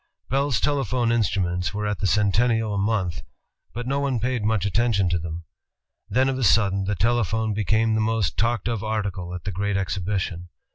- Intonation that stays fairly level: No, average, 3.3 semitones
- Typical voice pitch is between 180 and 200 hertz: No, low, 105 Hz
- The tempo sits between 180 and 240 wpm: Yes, average, 185 wpm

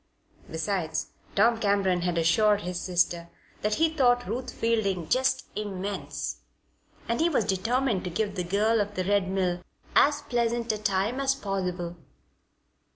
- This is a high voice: Yes, high, 205 Hz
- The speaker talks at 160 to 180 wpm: No, average, 150 wpm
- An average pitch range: Yes, average, 4.3 semitones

